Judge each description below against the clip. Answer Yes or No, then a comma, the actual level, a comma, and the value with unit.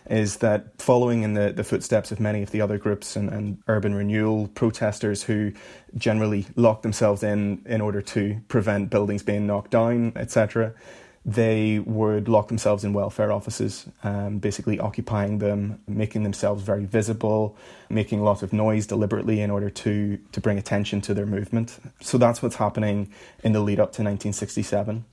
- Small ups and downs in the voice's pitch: Yes, narrow, 1.4 semitones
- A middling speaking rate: Yes, average, 175 wpm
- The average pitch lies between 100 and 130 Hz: Yes, low, 105 Hz